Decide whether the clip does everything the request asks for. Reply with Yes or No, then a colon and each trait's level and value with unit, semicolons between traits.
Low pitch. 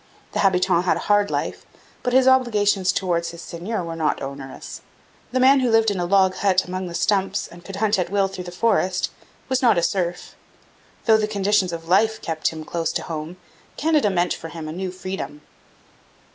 No: high, 190 Hz